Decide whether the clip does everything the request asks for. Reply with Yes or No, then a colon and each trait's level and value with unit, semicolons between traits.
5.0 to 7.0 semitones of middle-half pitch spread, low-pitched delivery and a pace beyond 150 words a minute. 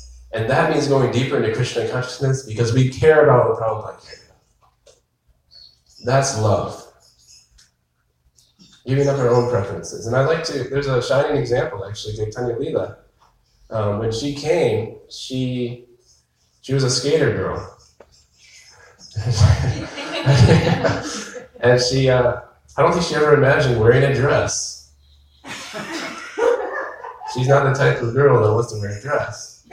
No: wide, 5.4 semitones; low, 120 Hz; slow, 135 wpm